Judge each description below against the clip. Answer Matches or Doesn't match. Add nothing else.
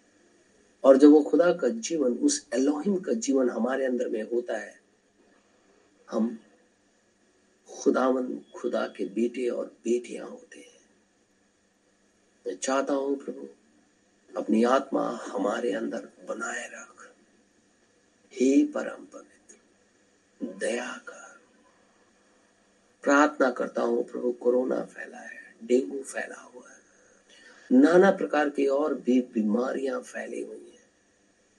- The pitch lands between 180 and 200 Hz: Doesn't match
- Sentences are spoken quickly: Doesn't match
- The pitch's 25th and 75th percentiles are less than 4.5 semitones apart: Matches